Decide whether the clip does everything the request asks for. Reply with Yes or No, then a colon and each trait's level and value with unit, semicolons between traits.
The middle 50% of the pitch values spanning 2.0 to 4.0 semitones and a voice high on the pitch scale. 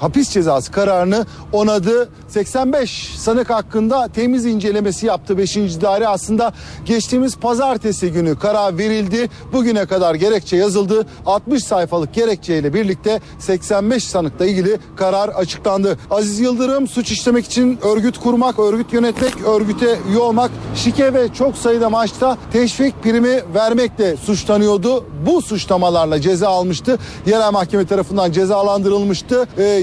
Yes: average, 3.5 semitones; high, 215 Hz